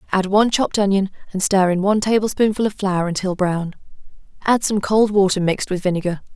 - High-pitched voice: Yes, high, 195 Hz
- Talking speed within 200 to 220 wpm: No, average, 190 wpm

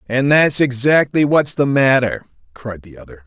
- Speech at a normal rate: Yes, average, 165 wpm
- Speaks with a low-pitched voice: Yes, low, 130 Hz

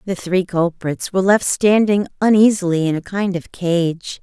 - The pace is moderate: Yes, average, 170 wpm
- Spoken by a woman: Yes, female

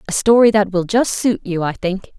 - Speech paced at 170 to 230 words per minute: No, fast, 245 wpm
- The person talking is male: No, female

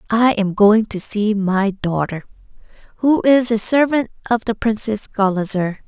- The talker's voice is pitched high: Yes, high, 215 Hz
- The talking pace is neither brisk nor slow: Yes, average, 155 wpm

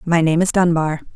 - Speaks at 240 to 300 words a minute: No, fast, 210 wpm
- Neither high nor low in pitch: Yes, medium, 165 Hz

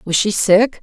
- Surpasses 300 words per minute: No, fast, 215 wpm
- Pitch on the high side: Yes, high, 205 Hz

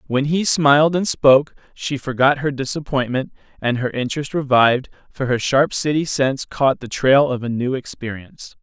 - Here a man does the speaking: Yes, male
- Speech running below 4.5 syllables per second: No, 5.1 syllables/s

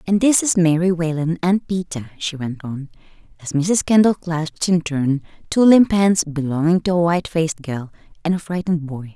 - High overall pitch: No, medium, 165 Hz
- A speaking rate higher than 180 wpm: Yes, average, 190 wpm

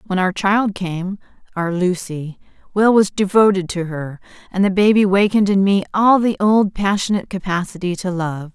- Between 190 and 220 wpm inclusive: No, average, 155 wpm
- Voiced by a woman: Yes, female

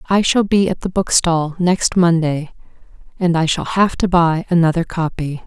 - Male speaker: No, female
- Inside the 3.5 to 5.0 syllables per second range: Yes, 4.5 syllables/s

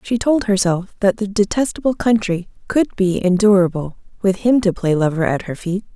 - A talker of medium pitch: No, high, 200 Hz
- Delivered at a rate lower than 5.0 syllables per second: No, 5.1 syllables/s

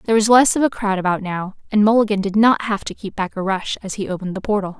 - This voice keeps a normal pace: No, fast, 290 wpm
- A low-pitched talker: No, high, 205 Hz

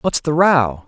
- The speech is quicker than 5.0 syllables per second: No, 3.6 syllables/s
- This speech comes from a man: Yes, male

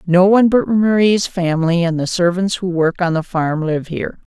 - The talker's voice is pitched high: No, medium, 180 Hz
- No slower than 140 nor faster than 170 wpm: No, fast, 205 wpm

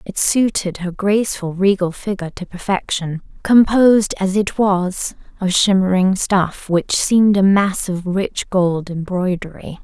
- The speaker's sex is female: Yes, female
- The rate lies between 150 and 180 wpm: No, average, 140 wpm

